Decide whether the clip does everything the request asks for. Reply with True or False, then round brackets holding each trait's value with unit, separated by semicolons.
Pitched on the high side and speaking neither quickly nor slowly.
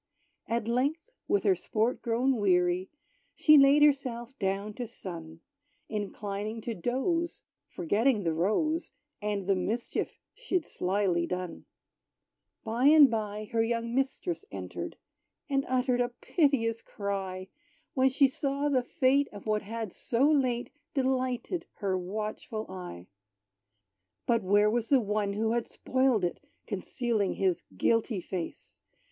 False (230 Hz; 130 wpm)